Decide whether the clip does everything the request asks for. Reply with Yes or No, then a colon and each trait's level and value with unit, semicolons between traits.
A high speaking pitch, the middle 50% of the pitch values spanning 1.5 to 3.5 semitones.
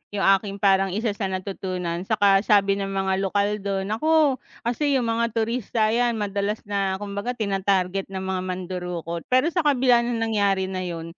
Yes: high, 200 Hz; average, 3.0 semitones